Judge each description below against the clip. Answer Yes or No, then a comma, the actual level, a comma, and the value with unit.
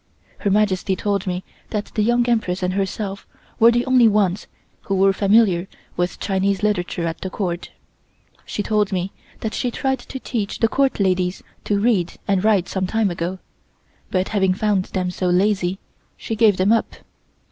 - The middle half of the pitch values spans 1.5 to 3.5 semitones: Yes, average, 2.8 semitones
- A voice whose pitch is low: No, high, 200 Hz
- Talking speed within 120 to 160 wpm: No, average, 175 wpm